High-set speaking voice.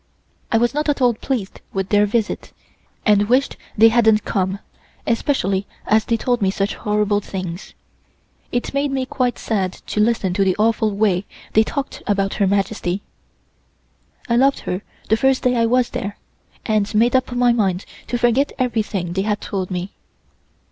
Yes: high, 215 Hz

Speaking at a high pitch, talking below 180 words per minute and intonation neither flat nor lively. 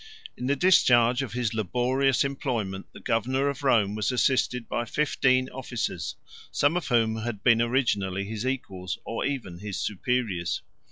No: low, 120 Hz; average, 160 wpm; average, 3.7 semitones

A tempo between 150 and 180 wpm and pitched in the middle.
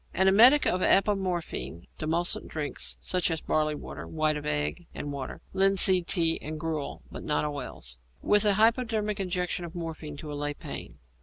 Yes: average, 170 wpm; medium, 165 Hz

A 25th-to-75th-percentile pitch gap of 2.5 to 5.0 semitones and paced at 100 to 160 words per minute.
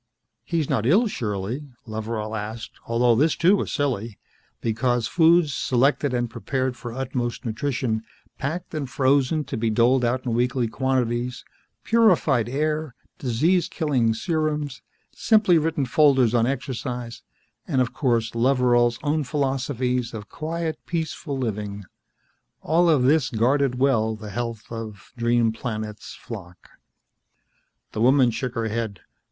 Yes: average, 3.9 semitones; slow, 135 wpm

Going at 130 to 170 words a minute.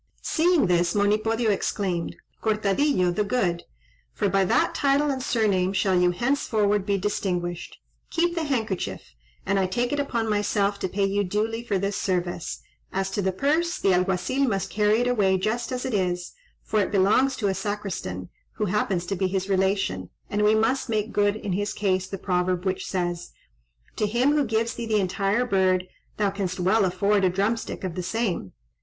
No: average, 185 wpm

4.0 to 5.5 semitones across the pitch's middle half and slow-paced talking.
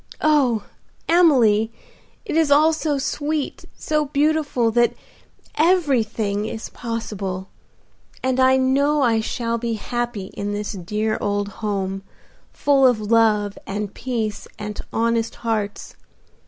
Yes: average, 4.7 semitones; slow, 120 wpm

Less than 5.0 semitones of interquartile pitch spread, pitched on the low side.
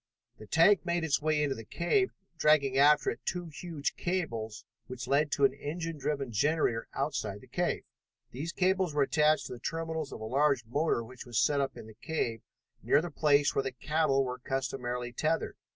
No: average, 4.3 semitones; medium, 145 Hz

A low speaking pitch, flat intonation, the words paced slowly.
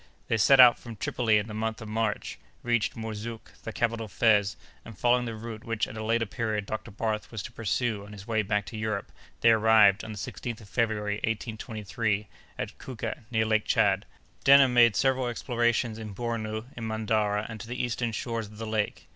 No: low, 110 Hz; narrow, 1.5 semitones; fast, 205 wpm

